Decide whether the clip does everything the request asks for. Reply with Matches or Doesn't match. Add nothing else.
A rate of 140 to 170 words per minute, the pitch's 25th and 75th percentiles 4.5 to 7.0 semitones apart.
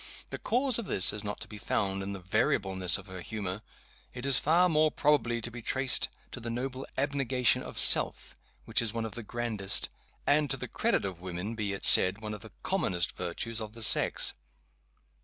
Doesn't match